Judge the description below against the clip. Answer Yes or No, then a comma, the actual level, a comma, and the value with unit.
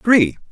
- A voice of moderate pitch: Yes, medium, 175 Hz